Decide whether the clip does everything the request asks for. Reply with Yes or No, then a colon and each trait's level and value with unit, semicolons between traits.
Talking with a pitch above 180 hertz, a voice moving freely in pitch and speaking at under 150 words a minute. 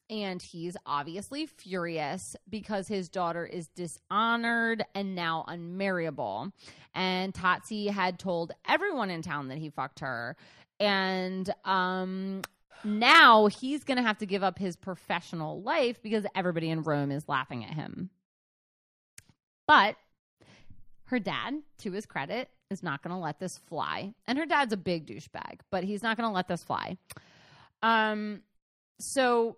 No: high, 190 Hz; average, 4.0 semitones; average, 140 wpm